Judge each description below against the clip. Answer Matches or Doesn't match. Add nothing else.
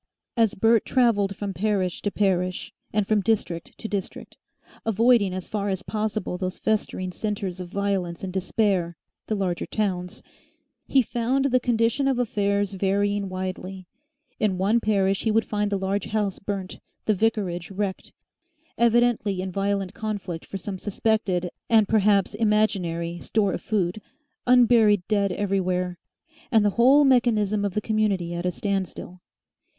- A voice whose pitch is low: Doesn't match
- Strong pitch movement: Doesn't match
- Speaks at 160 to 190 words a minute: Doesn't match